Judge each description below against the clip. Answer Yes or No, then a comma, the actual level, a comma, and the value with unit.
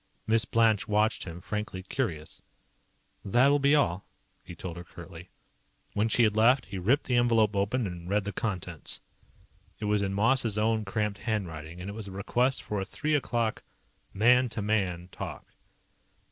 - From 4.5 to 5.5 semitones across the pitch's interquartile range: No, average, 3.4 semitones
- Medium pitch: No, low, 105 Hz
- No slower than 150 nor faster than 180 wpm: Yes, average, 175 wpm